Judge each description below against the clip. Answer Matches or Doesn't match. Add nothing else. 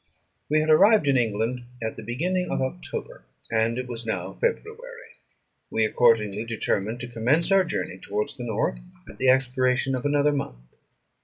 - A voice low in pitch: Matches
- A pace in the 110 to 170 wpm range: Matches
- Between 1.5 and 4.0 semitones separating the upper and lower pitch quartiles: Doesn't match